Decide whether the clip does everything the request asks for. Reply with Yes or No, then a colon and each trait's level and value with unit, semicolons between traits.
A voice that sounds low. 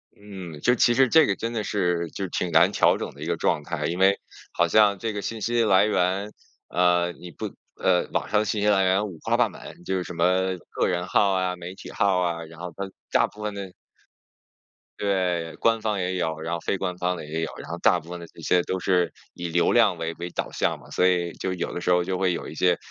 Yes: very low, 90 Hz